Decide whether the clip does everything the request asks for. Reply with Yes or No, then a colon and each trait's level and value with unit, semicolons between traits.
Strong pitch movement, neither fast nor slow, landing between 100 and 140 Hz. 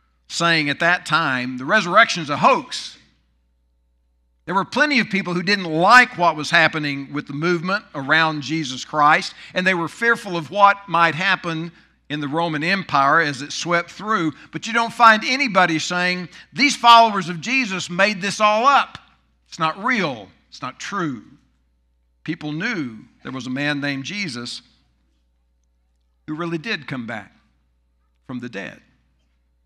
No: wide, 8.3 semitones; average, 160 wpm; medium, 160 Hz